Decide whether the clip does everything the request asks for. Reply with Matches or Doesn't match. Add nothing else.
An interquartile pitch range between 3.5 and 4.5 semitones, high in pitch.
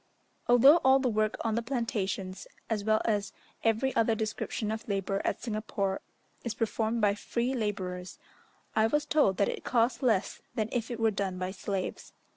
Doesn't match